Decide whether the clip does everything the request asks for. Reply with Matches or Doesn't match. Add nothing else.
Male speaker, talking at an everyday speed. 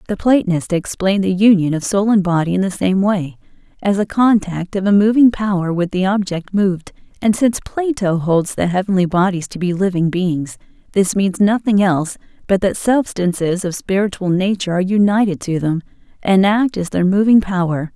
Doesn't match